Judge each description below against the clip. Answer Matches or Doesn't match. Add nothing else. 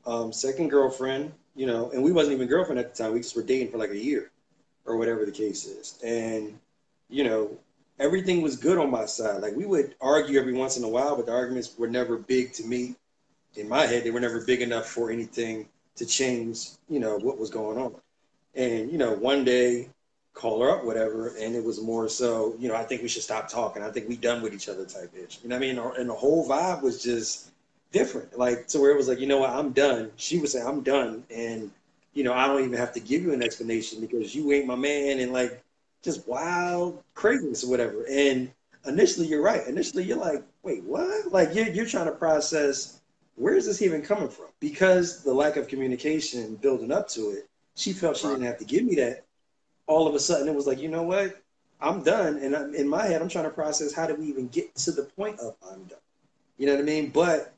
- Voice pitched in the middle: Doesn't match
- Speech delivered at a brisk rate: Matches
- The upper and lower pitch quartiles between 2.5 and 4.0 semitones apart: Doesn't match